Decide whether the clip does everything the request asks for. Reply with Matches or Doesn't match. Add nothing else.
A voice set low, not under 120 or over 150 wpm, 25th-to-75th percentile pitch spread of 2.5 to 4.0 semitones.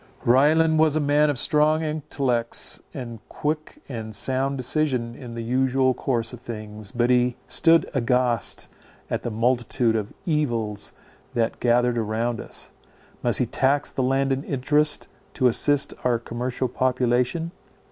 Matches